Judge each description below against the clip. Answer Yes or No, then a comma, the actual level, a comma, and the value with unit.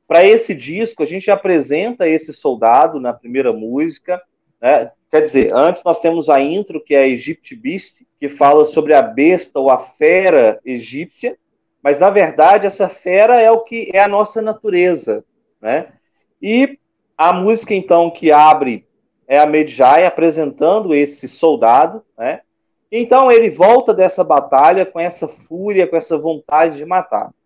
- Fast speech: No, average, 155 wpm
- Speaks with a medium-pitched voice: Yes, medium, 180 Hz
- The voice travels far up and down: Yes, wide, 6.3 semitones